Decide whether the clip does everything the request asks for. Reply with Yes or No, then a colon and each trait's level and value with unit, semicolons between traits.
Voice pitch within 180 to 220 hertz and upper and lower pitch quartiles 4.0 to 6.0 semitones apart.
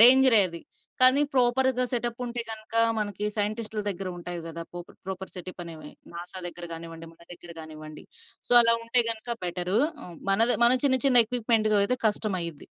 Yes: high, 210 Hz; wide, 5.5 semitones